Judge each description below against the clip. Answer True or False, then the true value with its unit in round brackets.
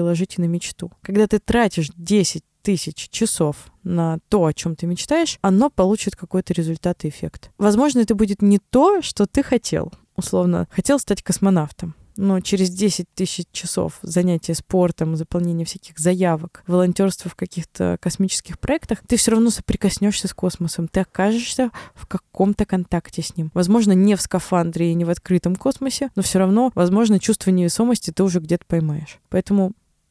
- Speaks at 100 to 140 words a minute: False (160 wpm)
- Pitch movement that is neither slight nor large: True (3.4 semitones)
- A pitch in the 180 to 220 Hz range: True (185 Hz)